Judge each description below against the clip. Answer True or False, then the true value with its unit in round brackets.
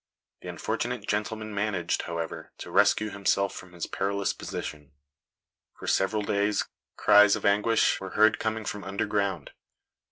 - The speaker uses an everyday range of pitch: False (1.7 semitones)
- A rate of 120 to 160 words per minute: True (135 wpm)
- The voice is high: False (100 Hz)